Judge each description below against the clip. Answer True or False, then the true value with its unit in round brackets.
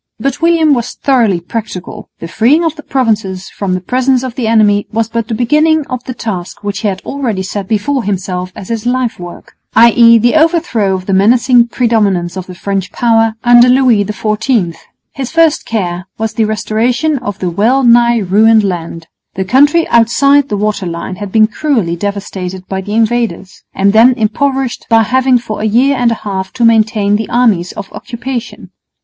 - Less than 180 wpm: False (185 wpm)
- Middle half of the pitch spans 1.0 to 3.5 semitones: False (4.0 semitones)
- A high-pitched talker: True (225 Hz)